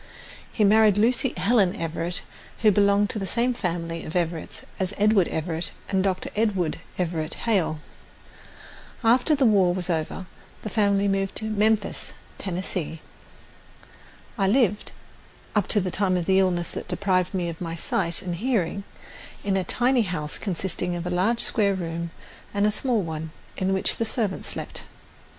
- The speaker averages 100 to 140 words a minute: No, average, 160 wpm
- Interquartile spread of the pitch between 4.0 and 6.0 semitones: No, average, 3.4 semitones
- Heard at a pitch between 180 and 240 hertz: Yes, high, 190 Hz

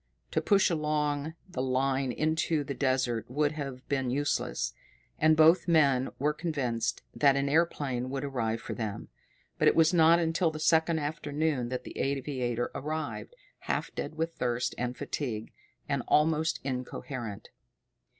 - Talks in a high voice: No, medium, 140 Hz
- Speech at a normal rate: Yes, average, 150 wpm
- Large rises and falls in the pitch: No, average, 3.7 semitones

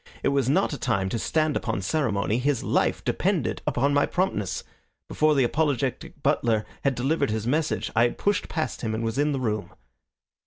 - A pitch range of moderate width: Yes, average, 4.8 semitones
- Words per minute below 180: No, average, 190 wpm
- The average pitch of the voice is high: No, low, 130 Hz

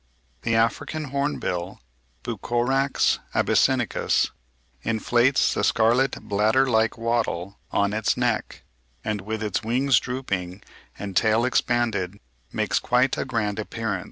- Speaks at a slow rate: Yes, slow, 115 wpm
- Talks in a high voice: No, low, 115 Hz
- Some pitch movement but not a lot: Yes, average, 3.2 semitones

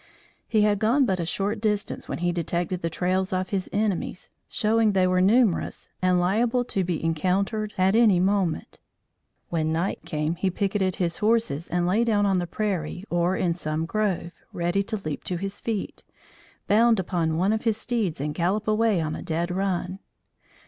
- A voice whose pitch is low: No, high, 190 Hz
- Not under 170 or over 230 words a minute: Yes, average, 185 wpm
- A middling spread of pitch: Yes, average, 3.5 semitones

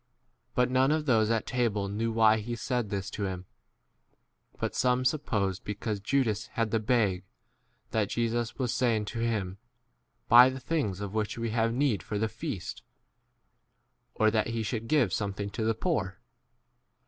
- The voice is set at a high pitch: No, low, 115 Hz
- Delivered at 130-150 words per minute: No, average, 170 wpm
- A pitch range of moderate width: Yes, average, 3.1 semitones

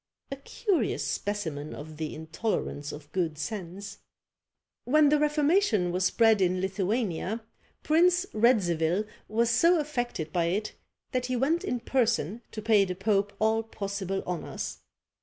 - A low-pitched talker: No, high, 210 Hz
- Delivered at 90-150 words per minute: Yes, average, 140 wpm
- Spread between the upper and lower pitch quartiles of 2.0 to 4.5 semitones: No, wide, 5.6 semitones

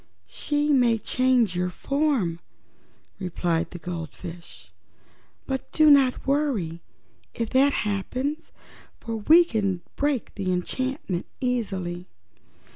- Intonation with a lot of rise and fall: Yes, wide, 7.4 semitones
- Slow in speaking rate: Yes, slow, 105 wpm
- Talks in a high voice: Yes, high, 225 Hz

